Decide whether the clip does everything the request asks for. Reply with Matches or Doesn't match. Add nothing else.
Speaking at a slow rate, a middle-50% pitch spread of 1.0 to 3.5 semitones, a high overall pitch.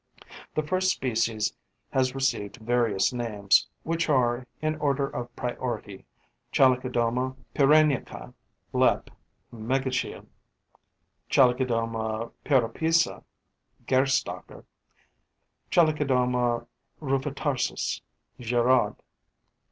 Doesn't match